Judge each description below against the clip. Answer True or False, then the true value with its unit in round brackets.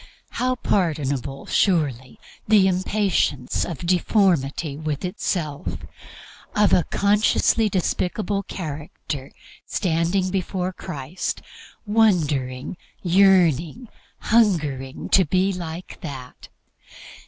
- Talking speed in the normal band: False (85 wpm)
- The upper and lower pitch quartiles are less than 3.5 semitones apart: False (5.2 semitones)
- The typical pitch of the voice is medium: True (175 Hz)